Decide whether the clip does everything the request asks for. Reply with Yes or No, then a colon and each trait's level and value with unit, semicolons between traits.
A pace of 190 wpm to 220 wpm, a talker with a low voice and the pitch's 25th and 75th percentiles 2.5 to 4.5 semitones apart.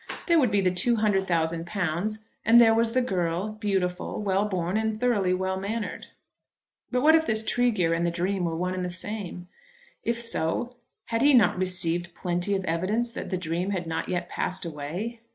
No: average, 195 wpm; high, 190 Hz; average, 4.0 semitones